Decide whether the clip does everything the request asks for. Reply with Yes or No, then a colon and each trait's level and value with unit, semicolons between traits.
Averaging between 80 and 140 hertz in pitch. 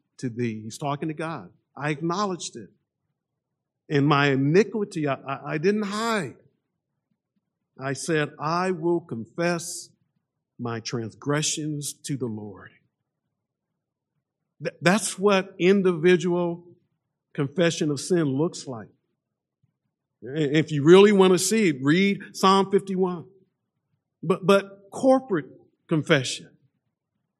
No: medium, 160 Hz